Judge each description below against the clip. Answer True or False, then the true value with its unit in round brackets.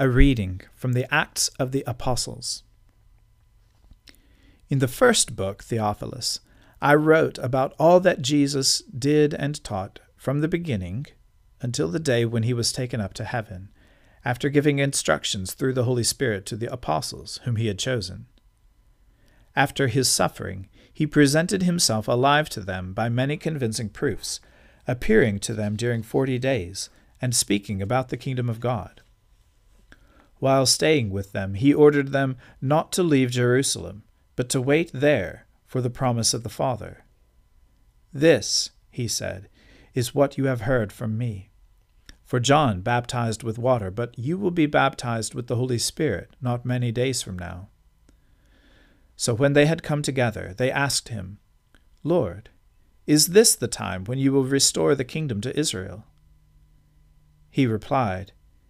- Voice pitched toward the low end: True (120 Hz)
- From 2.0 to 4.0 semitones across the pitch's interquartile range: False (4.9 semitones)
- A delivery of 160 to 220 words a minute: False (150 wpm)